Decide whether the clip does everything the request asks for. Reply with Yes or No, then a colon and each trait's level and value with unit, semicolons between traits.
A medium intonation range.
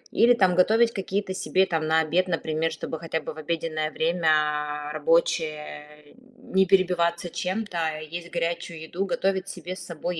Yes: average, 3.0 semitones